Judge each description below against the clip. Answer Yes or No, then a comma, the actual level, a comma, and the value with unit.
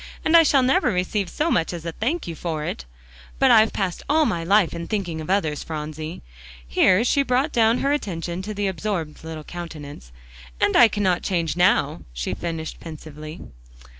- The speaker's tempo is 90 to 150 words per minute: No, average, 185 wpm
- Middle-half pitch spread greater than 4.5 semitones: Yes, average, 5.2 semitones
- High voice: No, medium, 175 Hz